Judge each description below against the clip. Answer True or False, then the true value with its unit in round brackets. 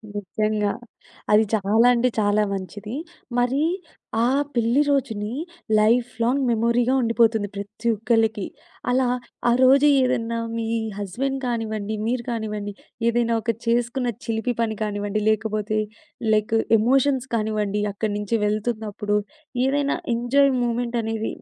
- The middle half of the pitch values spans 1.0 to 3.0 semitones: True (2.4 semitones)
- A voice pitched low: False (225 Hz)